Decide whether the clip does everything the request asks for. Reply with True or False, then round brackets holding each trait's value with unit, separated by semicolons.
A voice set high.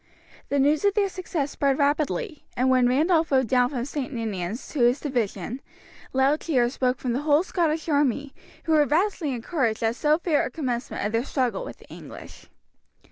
True (275 Hz)